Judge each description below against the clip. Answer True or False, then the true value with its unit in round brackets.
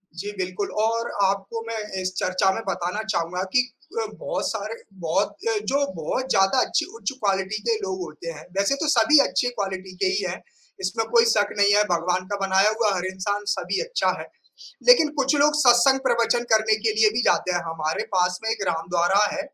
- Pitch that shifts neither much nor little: True (4.5 semitones)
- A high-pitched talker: True (205 Hz)